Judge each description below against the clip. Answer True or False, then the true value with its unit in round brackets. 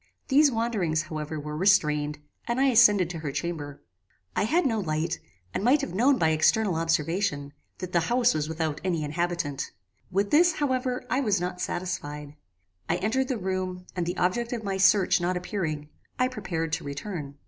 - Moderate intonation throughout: False (6.1 semitones)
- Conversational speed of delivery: True (180 wpm)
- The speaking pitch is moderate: True (180 Hz)